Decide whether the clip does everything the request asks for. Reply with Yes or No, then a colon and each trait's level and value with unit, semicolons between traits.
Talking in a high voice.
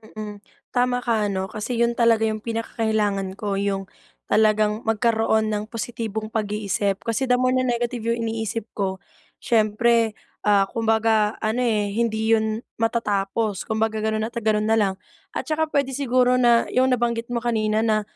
Yes: high, 220 Hz